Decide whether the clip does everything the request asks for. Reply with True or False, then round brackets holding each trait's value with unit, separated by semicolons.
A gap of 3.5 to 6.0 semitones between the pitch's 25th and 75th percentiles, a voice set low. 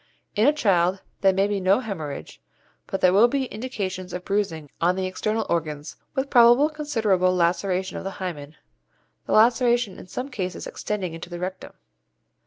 False (4.1 semitones; 190 Hz)